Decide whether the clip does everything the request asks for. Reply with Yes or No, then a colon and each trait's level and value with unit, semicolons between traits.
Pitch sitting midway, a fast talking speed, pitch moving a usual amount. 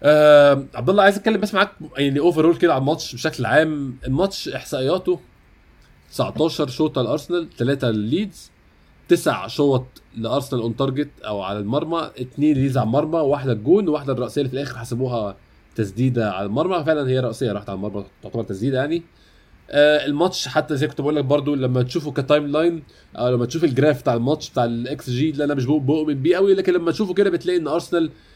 Yes: medium, 145 Hz; fast, 180 wpm; average, 4.5 semitones